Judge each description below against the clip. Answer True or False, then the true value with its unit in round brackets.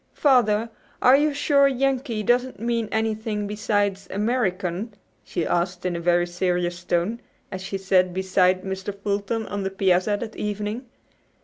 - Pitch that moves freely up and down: False (3.7 semitones)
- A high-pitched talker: True (205 Hz)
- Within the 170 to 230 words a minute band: False (145 wpm)